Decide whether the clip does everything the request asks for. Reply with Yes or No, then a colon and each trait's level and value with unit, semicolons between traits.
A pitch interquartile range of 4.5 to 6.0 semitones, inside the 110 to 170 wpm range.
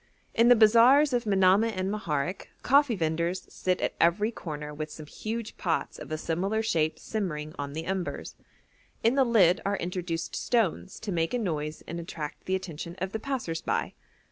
No: average, 5.2 semitones; average, 180 wpm